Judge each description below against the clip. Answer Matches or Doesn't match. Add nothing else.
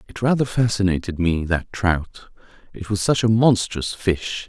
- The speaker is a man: Matches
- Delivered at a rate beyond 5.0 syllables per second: Doesn't match